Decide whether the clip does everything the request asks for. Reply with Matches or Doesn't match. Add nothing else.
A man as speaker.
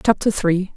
Doesn't match